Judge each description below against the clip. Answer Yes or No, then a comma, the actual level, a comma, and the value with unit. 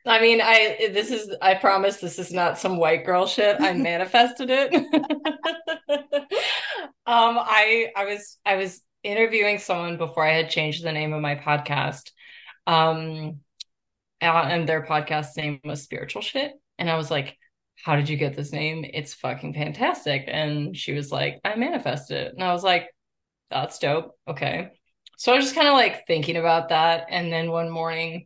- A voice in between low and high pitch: Yes, medium, 170 Hz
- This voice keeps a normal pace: Yes, average, 175 wpm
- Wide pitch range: Yes, wide, 6.3 semitones